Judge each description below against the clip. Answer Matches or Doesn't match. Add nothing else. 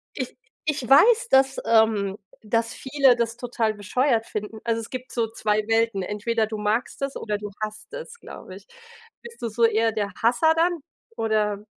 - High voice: Matches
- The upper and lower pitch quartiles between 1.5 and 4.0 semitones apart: Matches